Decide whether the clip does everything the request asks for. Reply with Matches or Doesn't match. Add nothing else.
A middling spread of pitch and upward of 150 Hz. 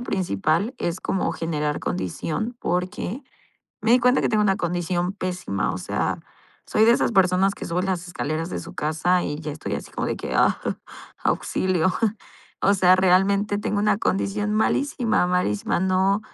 Matches